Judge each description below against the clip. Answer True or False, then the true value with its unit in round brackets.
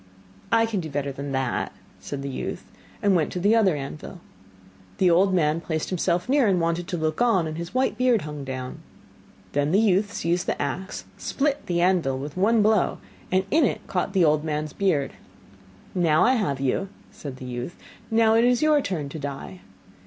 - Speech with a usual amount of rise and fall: False (5.7 semitones)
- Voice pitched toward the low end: False (175 Hz)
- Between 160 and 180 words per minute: False (195 wpm)